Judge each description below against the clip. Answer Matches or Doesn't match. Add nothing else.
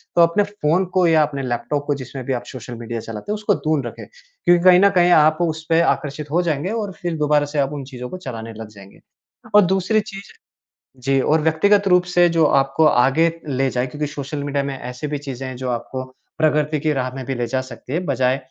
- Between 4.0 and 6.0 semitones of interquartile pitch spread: Matches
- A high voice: Doesn't match